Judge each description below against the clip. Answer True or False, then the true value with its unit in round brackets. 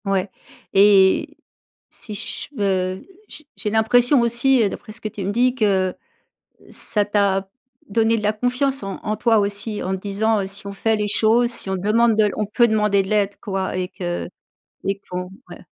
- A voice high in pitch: True (210 Hz)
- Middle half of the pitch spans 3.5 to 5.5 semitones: False (2.5 semitones)